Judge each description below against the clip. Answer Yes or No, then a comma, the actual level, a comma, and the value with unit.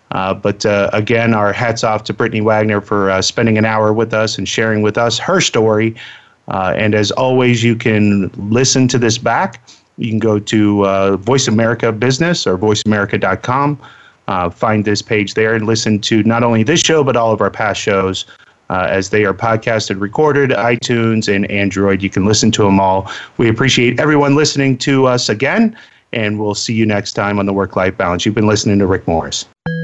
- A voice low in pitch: Yes, low, 110 Hz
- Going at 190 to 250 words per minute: Yes, average, 200 wpm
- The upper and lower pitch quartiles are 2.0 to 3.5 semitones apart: Yes, narrow, 2.6 semitones